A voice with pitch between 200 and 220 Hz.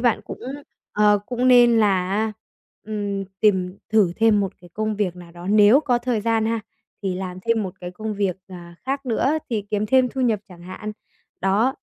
Yes: high, 210 Hz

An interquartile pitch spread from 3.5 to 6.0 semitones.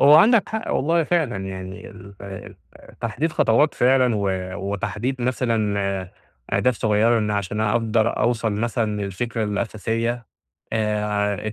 No: average, 3.1 semitones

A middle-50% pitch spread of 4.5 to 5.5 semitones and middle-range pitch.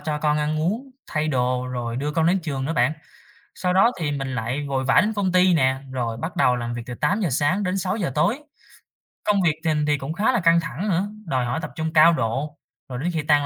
Yes: average, 5.2 semitones; medium, 150 Hz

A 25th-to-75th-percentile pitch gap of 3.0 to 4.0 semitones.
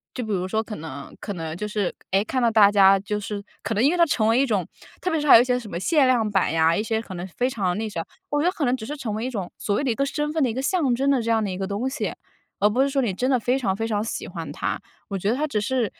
No: average, 4.6 semitones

